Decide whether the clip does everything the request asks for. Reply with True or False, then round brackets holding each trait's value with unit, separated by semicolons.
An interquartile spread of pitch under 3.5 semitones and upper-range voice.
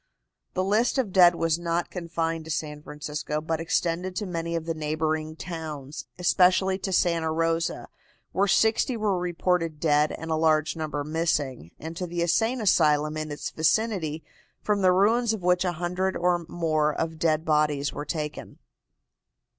False (2.6 semitones; 165 Hz)